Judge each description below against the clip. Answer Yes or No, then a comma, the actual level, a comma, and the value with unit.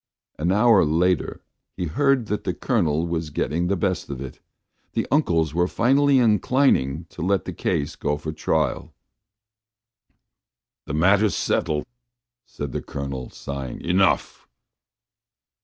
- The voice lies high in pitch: No, very low, 85 Hz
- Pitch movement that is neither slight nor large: No, wide, 5.8 semitones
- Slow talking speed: Yes, slow, 130 wpm